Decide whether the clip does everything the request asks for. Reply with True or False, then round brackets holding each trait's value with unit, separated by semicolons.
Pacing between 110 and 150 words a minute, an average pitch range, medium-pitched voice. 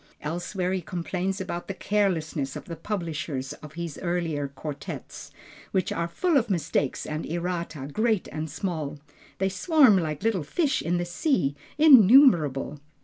True (145 wpm; 4.1 semitones; 175 Hz)